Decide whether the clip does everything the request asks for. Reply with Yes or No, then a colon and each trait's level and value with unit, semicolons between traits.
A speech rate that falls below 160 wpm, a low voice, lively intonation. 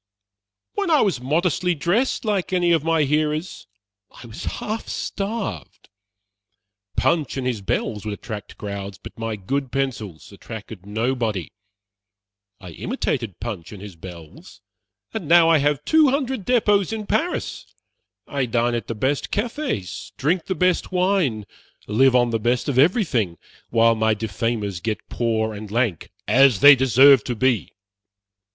Yes: average, 145 wpm; low, 125 Hz; wide, 8.2 semitones